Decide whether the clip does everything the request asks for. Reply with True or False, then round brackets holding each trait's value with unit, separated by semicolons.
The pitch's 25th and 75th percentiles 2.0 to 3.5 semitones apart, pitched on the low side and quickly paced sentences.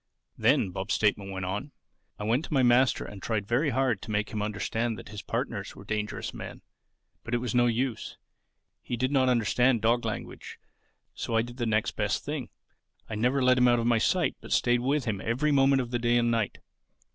True (2.9 semitones; 120 Hz; 215 wpm)